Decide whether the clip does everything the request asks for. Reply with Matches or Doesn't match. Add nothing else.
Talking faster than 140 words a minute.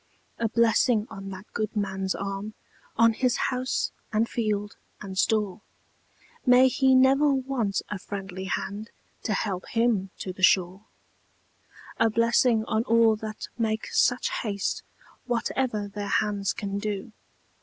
Doesn't match